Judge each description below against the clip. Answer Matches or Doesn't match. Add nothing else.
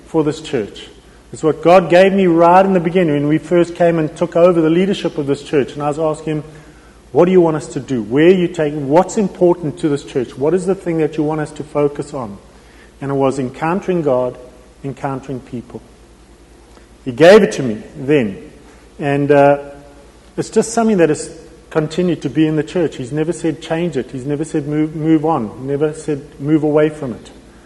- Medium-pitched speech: Matches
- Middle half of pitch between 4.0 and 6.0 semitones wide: Doesn't match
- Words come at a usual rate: Doesn't match